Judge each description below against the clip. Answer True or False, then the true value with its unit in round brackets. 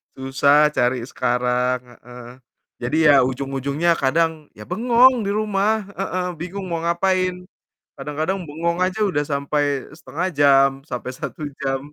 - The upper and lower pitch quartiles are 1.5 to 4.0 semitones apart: False (5.2 semitones)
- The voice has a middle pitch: True (150 Hz)